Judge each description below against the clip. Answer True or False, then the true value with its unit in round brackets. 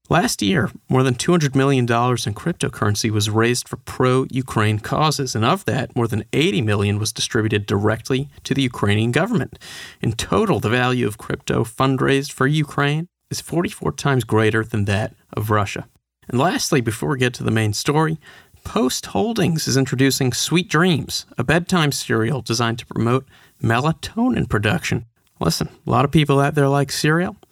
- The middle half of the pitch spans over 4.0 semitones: True (4.4 semitones)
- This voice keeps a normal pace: True (170 wpm)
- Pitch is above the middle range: False (130 Hz)